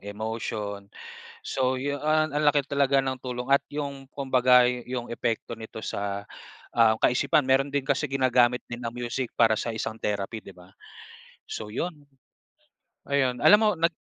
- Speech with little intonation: No, average, 3.8 semitones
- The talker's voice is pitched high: No, low, 125 Hz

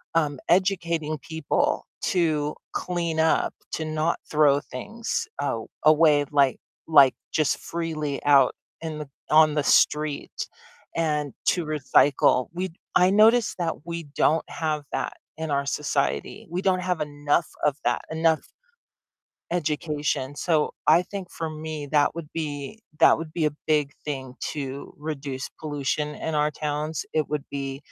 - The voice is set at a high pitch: No, medium, 155 Hz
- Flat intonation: Yes, narrow, 2.2 semitones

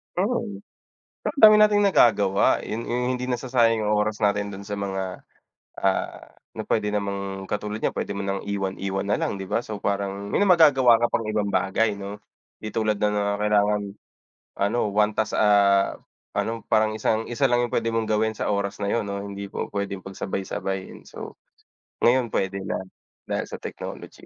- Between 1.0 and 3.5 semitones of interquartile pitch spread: Yes, narrow, 2.4 semitones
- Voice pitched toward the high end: No, low, 105 Hz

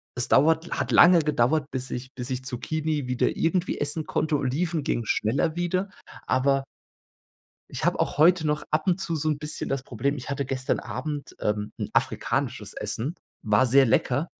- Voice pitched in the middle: Yes, medium, 145 Hz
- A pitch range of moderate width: Yes, average, 3.5 semitones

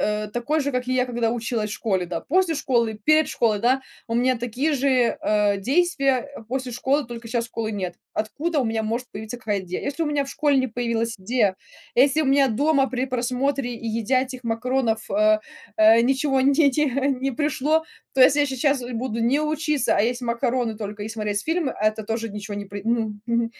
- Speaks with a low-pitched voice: No, high, 245 Hz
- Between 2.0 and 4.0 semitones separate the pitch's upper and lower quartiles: Yes, average, 3.7 semitones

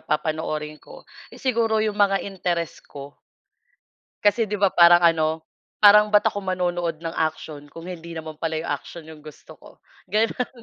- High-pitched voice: No, medium, 175 Hz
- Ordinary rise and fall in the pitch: Yes, average, 4.7 semitones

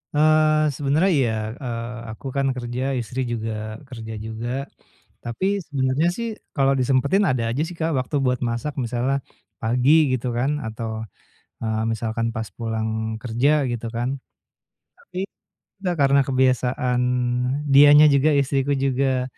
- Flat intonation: No, average, 3.4 semitones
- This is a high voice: No, low, 130 Hz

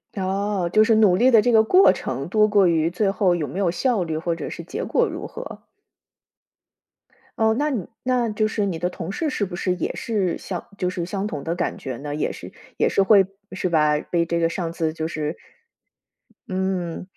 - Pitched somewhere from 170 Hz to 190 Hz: Yes, medium, 185 Hz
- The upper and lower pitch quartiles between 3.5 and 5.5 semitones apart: Yes, average, 4.0 semitones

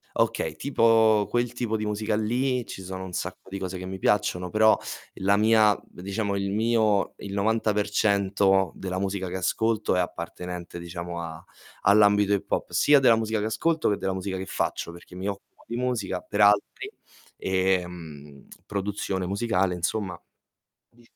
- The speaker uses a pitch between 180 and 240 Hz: No, low, 100 Hz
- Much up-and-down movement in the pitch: No, average, 2.8 semitones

